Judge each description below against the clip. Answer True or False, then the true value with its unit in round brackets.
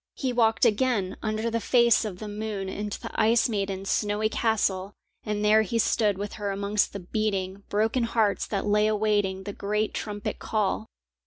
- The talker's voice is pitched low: False (210 Hz)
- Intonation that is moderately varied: False (1.6 semitones)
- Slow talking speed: False (175 wpm)